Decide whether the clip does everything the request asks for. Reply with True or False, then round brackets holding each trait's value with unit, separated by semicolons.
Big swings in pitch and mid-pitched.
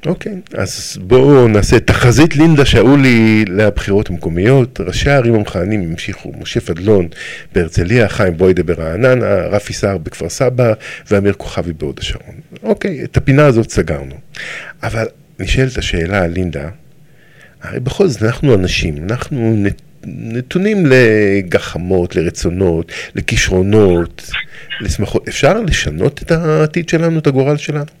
False (7.2 semitones; 110 Hz)